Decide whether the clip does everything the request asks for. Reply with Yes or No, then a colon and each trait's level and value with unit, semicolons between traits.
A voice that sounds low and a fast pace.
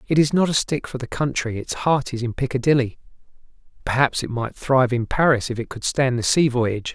Yes: low, 130 Hz; fast, 225 wpm